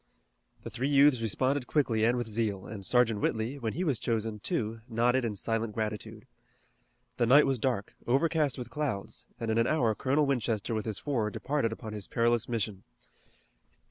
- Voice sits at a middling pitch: No, low, 115 Hz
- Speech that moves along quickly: No, average, 175 wpm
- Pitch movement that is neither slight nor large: Yes, average, 3.2 semitones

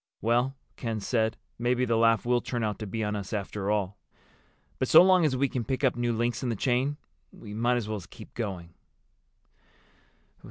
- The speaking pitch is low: Yes, low, 115 Hz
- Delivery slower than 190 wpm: No, average, 200 wpm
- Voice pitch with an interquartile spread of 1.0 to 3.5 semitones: Yes, average, 2.8 semitones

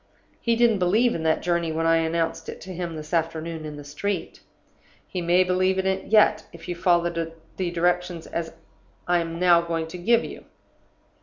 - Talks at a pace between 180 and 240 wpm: Yes, average, 185 wpm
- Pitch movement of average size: No, narrow, 2.1 semitones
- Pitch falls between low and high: Yes, medium, 175 Hz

